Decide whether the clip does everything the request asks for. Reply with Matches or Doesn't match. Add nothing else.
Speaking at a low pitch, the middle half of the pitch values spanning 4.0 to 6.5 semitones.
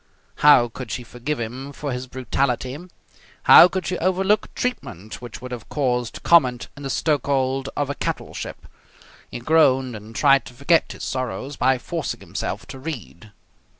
Doesn't match